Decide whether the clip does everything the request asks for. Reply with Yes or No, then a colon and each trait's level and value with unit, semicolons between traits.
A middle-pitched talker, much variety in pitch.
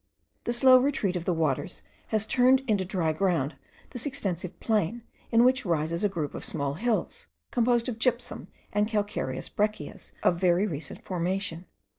No: high, 200 Hz; wide, 5.8 semitones